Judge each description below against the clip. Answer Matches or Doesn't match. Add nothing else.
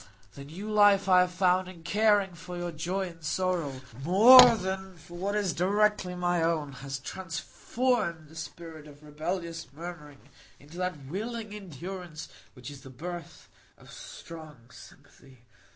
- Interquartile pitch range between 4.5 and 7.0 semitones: Doesn't match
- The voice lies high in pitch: Doesn't match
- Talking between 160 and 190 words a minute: Doesn't match